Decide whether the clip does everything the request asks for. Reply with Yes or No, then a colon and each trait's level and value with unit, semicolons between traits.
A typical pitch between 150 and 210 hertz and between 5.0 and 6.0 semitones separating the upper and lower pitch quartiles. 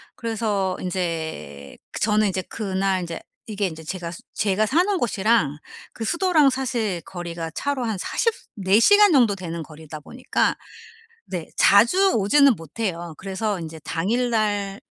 Yes: high, 200 Hz; average, 5.3 semitones